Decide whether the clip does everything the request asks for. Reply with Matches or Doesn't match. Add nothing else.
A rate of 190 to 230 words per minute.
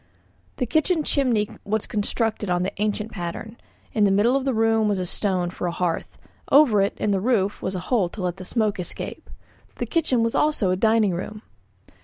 Matches